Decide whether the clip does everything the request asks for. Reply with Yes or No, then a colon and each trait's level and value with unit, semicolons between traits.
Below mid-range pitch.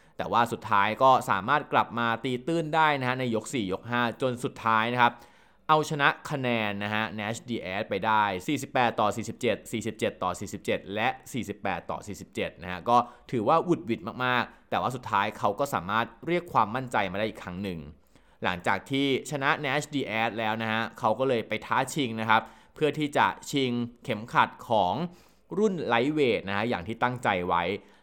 Yes: low, 120 Hz